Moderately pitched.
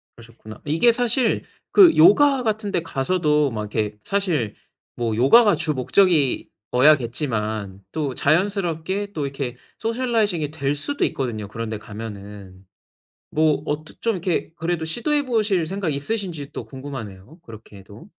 Yes: medium, 150 Hz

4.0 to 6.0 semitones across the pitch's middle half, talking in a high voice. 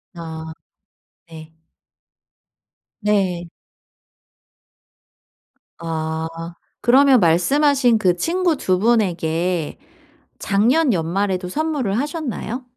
No: wide, 7.6 semitones; high, 195 Hz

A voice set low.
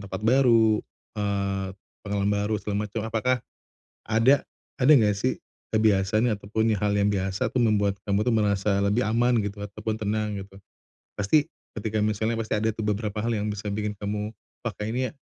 Yes: low, 105 Hz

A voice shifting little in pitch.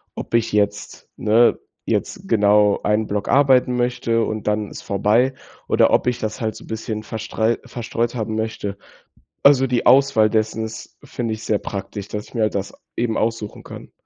Yes: narrow, 2.1 semitones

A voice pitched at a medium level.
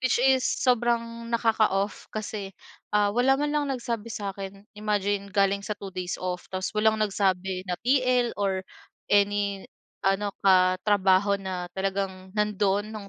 No: high, 205 Hz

